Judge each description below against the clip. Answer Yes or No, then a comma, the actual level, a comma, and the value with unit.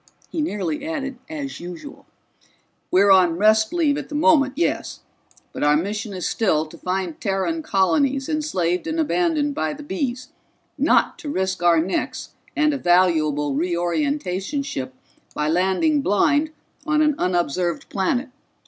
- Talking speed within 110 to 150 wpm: Yes, average, 145 wpm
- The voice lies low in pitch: No, high, 205 Hz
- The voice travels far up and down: Yes, wide, 8.8 semitones